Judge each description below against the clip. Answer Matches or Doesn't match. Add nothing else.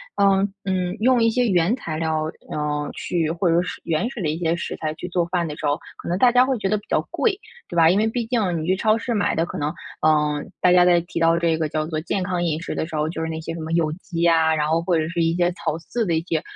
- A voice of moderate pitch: Matches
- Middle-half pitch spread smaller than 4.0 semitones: Matches